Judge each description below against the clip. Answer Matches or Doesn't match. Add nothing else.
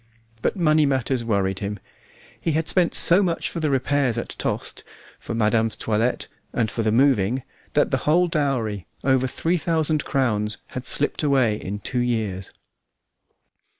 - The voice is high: Doesn't match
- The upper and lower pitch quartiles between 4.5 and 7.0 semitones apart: Matches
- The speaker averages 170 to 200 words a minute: Doesn't match